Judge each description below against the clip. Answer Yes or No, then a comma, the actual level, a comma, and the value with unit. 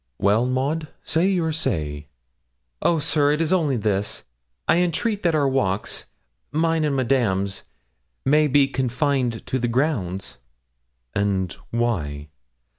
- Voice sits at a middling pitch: No, low, 130 Hz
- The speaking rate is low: Yes, slow, 125 wpm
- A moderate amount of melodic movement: No, wide, 7.2 semitones